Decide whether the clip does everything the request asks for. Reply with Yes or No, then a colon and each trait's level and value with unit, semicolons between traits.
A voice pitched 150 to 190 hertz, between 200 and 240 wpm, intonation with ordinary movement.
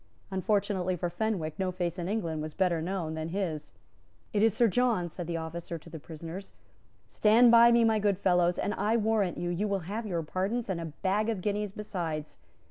Yes: medium, 185 Hz; fast, 205 wpm; average, 3.8 semitones